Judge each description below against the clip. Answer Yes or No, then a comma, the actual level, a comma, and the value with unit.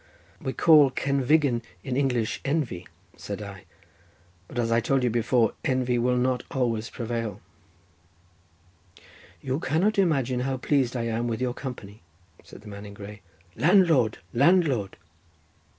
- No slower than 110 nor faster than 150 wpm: Yes, slow, 135 wpm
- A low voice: Yes, low, 125 Hz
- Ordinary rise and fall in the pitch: Yes, average, 3.1 semitones